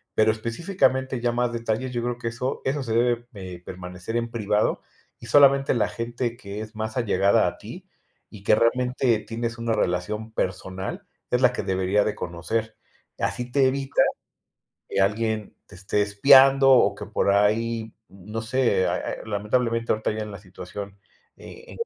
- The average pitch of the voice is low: Yes, low, 115 Hz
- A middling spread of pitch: Yes, average, 3.2 semitones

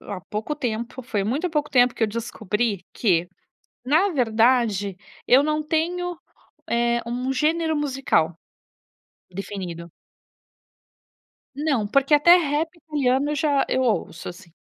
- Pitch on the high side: Yes, very high, 250 Hz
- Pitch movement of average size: No, wide, 6.0 semitones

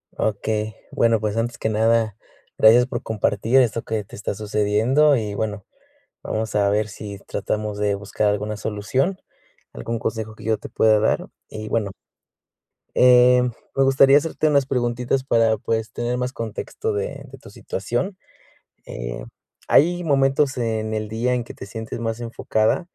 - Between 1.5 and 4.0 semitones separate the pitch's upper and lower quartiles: Yes, average, 2.8 semitones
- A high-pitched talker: No, low, 110 Hz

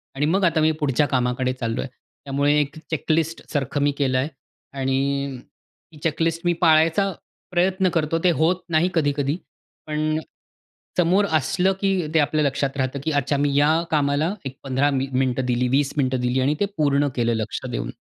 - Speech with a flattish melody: No, average, 3.1 semitones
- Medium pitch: Yes, medium, 145 Hz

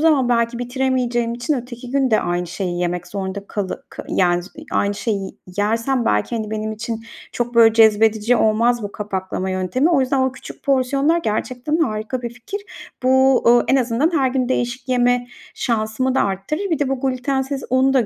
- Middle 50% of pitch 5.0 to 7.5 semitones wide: No, average, 3.6 semitones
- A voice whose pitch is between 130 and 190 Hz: No, high, 240 Hz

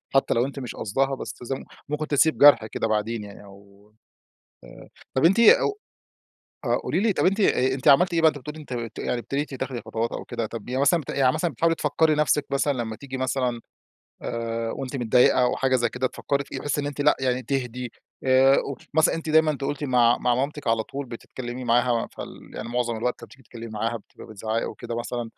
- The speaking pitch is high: No, low, 130 Hz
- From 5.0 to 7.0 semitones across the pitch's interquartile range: No, average, 3.5 semitones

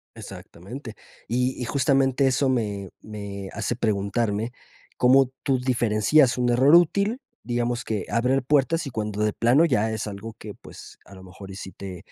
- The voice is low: Yes, low, 120 Hz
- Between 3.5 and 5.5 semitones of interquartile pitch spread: Yes, average, 4.2 semitones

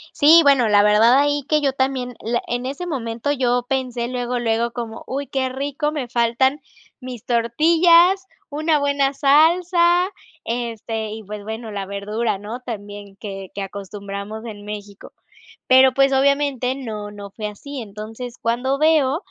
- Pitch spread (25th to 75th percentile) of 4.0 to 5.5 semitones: Yes, average, 4.4 semitones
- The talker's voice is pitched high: Yes, high, 245 Hz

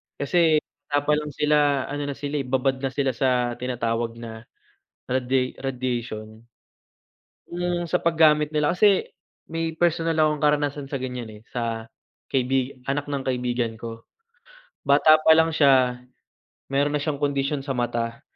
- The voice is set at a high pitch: No, low, 135 Hz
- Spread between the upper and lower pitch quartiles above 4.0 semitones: No, average, 3.3 semitones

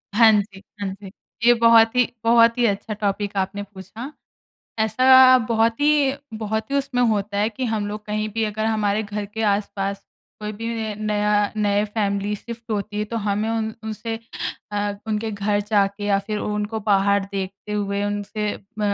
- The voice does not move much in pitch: Yes, narrow, 1.7 semitones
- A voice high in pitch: Yes, high, 210 Hz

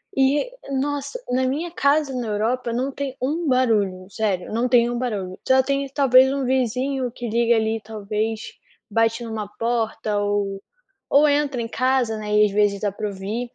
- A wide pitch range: No, average, 3.9 semitones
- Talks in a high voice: Yes, high, 235 Hz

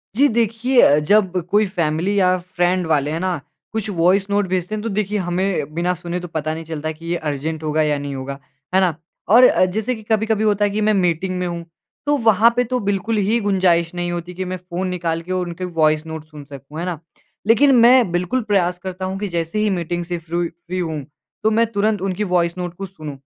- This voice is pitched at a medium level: Yes, medium, 180 Hz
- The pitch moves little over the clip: No, average, 3.7 semitones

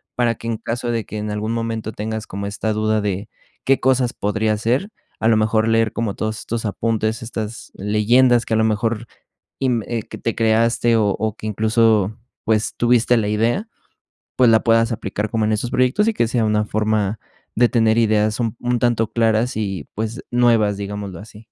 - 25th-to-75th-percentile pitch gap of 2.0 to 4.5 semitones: No, narrow, 1.6 semitones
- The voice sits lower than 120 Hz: Yes, low, 110 Hz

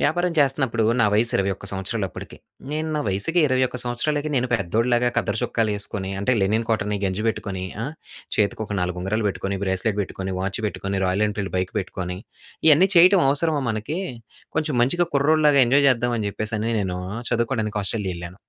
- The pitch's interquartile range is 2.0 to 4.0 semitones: No, average, 5.3 semitones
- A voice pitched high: No, low, 110 Hz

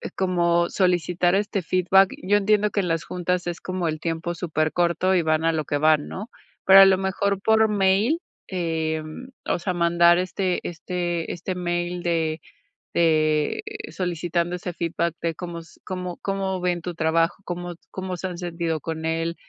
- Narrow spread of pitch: Yes, narrow, 2.1 semitones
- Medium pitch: Yes, medium, 175 Hz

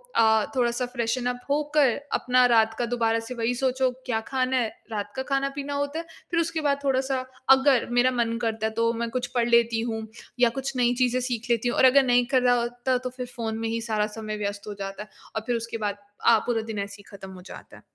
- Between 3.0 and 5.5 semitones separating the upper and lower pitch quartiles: No, narrow, 2.4 semitones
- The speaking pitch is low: No, high, 240 Hz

